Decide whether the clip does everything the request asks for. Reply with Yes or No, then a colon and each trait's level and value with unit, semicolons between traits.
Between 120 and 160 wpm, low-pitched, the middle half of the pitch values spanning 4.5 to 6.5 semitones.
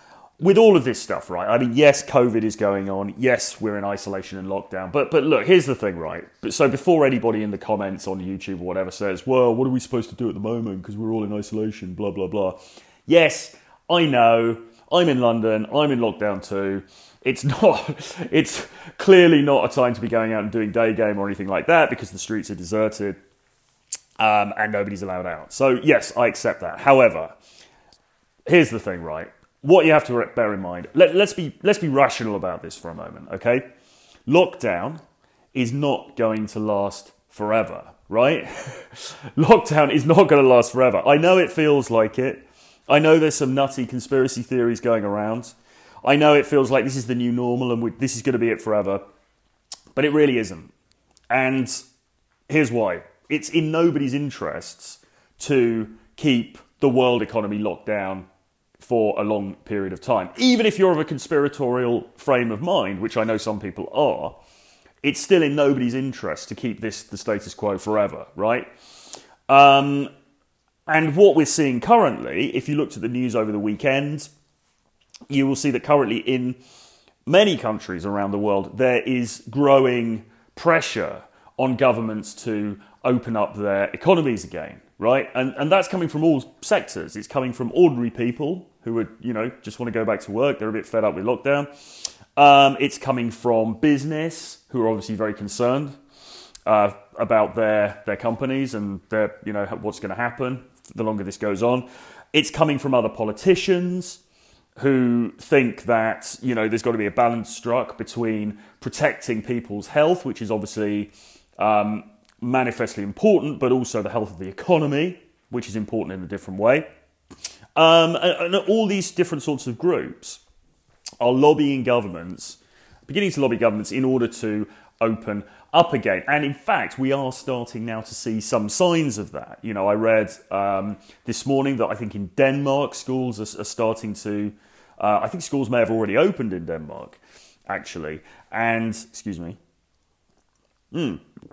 No: average, 180 wpm; low, 120 Hz; average, 4.8 semitones